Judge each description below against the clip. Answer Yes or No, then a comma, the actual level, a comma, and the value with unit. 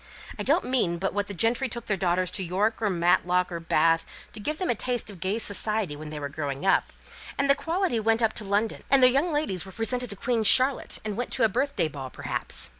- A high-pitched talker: Yes, high, 210 Hz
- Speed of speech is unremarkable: No, fast, 245 wpm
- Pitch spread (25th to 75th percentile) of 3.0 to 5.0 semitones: No, wide, 5.6 semitones